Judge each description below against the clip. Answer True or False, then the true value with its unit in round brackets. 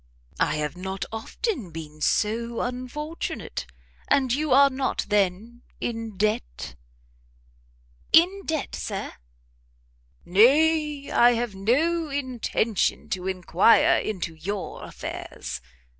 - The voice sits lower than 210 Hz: False (230 Hz)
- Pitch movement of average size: False (6.5 semitones)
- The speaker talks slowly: True (100 wpm)